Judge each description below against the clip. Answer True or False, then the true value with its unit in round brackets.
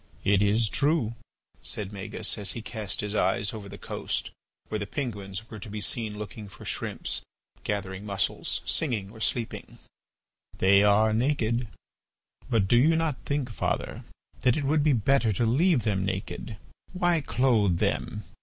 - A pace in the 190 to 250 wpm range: False (160 wpm)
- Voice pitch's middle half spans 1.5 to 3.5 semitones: False (4.0 semitones)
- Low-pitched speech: True (110 Hz)